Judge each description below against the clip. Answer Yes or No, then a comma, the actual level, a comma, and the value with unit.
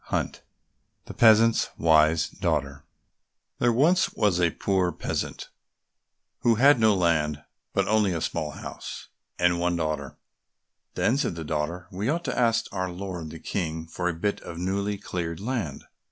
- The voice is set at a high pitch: No, very low, 90 Hz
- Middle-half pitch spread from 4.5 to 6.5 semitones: Yes, average, 4.9 semitones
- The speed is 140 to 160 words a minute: Yes, average, 155 wpm